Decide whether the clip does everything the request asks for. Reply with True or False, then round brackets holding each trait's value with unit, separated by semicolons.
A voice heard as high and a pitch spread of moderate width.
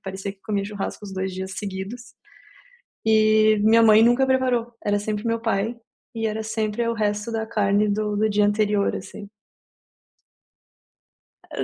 False (215 Hz; 1.7 semitones)